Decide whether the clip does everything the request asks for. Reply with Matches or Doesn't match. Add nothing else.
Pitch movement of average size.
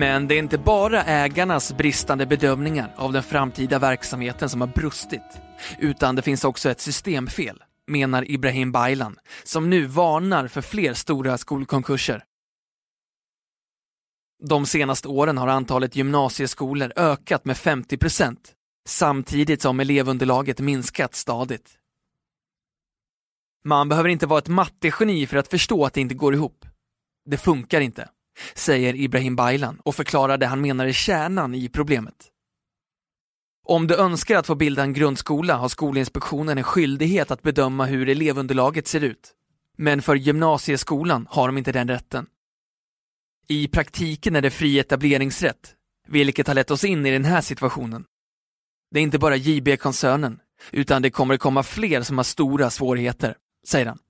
Doesn't match